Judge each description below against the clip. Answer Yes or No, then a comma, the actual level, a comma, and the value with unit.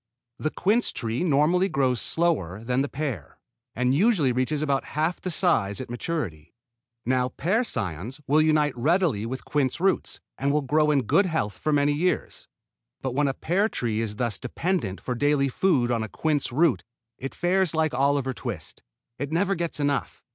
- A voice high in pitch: No, medium, 140 Hz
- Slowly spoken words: No, average, 175 wpm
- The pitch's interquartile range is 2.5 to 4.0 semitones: No, average, 4.8 semitones